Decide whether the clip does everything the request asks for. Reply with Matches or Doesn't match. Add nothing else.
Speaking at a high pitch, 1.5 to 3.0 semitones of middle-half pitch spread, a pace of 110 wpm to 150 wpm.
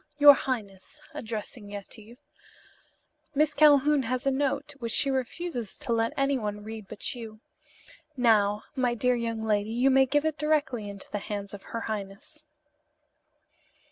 Doesn't match